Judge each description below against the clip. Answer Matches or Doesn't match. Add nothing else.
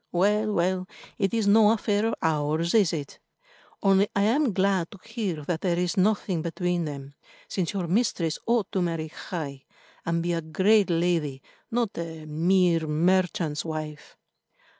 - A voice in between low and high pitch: Matches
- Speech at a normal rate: Matches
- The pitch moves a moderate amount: Matches